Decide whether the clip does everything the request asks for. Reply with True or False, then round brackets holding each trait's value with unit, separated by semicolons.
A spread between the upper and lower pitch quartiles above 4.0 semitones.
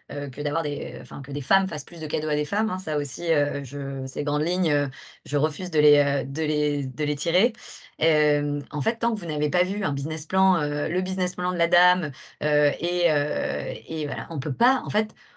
False (3.6 semitones)